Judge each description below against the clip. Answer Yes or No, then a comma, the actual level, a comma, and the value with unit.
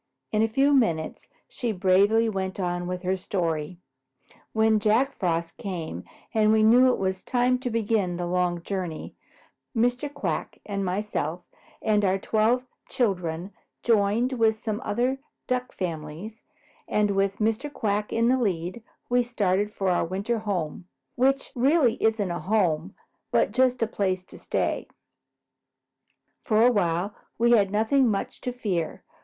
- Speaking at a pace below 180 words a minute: Yes, average, 150 wpm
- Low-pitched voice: No, high, 210 Hz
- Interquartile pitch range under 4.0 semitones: No, average, 4.3 semitones